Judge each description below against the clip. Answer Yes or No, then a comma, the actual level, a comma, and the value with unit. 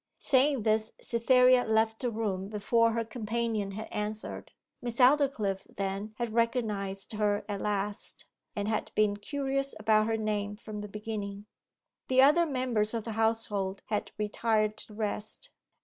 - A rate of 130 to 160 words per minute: Yes, average, 150 wpm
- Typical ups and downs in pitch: No, narrow, 2.1 semitones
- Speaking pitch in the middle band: No, high, 220 Hz